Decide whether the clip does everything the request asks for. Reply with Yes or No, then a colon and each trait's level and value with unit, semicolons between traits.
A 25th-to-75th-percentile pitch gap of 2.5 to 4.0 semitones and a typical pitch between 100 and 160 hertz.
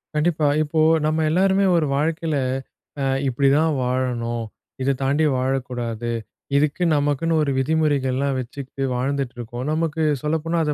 Yes: average, 3.5 semitones; medium, 140 Hz